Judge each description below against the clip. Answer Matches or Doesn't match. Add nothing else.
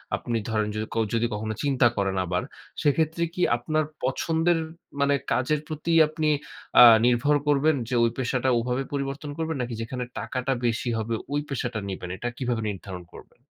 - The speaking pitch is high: Doesn't match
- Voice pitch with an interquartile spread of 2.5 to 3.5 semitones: Doesn't match